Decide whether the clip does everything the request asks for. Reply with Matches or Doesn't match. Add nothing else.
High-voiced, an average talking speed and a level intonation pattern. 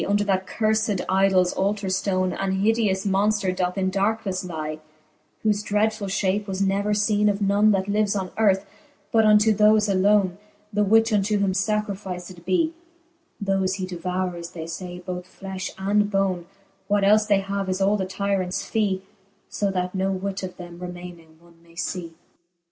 Matches